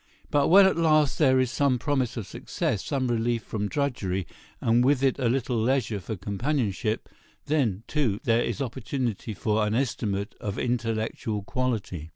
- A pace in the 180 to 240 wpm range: No, average, 160 wpm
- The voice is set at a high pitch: No, low, 120 Hz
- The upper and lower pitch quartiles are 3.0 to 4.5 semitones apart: Yes, average, 4.0 semitones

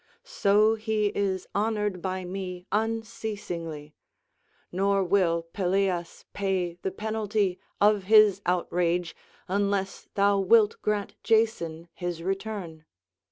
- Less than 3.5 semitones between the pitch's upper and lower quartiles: Yes, average, 2.9 semitones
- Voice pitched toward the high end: Yes, high, 195 Hz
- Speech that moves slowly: Yes, slow, 105 wpm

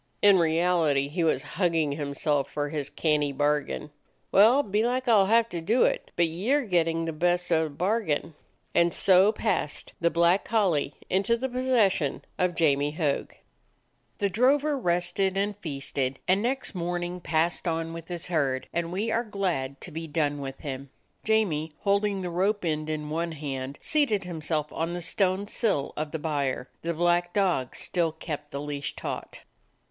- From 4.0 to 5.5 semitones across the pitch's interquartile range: Yes, average, 4.7 semitones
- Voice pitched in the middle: Yes, medium, 170 Hz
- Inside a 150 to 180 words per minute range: Yes, average, 175 wpm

